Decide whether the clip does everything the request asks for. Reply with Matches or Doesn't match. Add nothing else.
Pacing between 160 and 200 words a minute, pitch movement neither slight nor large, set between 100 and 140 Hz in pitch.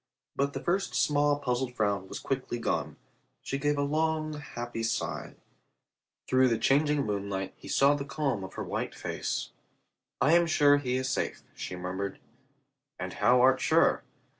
Matches